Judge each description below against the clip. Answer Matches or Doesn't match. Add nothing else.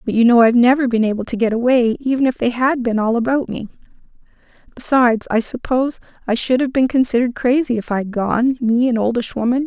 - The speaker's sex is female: Matches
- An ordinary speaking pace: Doesn't match